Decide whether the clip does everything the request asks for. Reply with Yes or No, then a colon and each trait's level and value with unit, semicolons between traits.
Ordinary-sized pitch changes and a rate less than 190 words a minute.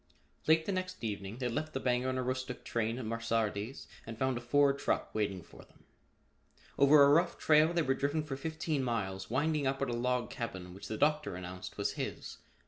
No: average, 4.4 semitones; fast, 205 wpm